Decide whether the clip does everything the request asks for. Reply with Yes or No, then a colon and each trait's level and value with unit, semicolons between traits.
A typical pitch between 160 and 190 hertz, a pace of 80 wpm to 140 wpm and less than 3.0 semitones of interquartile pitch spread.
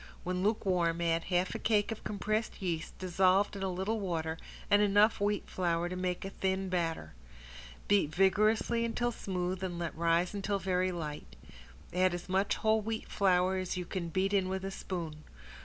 No: medium, 185 Hz; average, 180 wpm; narrow, 2.4 semitones